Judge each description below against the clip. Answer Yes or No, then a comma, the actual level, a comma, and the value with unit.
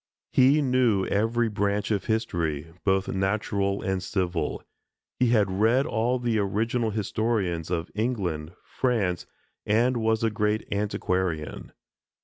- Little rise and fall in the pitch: No, average, 3.5 semitones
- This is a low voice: Yes, low, 105 Hz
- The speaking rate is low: Yes, slow, 125 wpm